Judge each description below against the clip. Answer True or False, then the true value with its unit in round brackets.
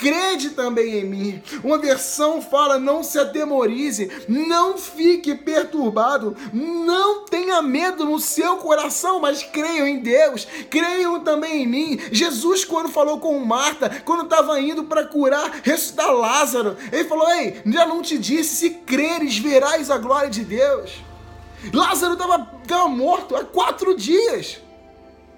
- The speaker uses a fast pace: False (140 wpm)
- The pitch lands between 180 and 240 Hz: False (300 Hz)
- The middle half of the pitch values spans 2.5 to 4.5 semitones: True (3.6 semitones)